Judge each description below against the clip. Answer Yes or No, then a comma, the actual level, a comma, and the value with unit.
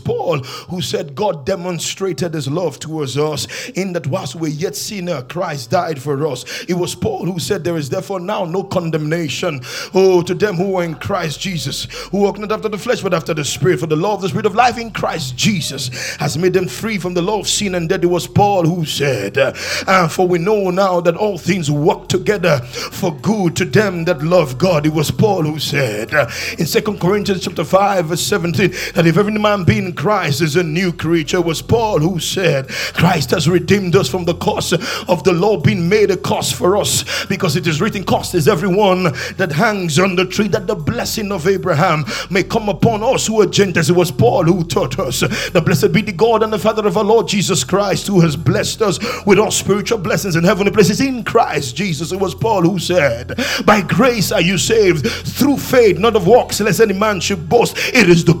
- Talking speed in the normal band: No, fast, 220 wpm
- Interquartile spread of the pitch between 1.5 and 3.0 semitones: No, average, 3.5 semitones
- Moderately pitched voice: Yes, medium, 180 Hz